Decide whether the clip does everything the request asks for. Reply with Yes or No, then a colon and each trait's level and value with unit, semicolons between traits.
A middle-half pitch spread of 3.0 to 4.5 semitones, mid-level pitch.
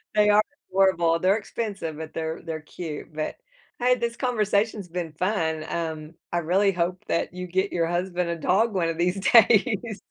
Yes: average, 3.8 semitones; medium, 180 Hz